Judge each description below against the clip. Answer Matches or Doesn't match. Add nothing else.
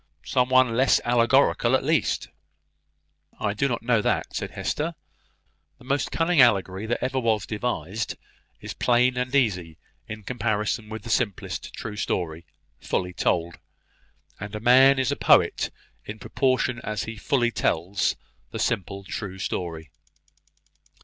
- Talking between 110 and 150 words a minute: Matches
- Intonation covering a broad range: Doesn't match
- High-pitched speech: Doesn't match